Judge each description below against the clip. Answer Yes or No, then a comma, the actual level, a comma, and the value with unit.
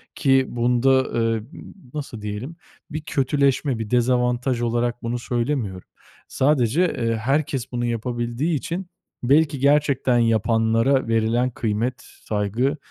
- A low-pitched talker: Yes, low, 120 Hz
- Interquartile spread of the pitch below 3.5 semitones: Yes, average, 3.0 semitones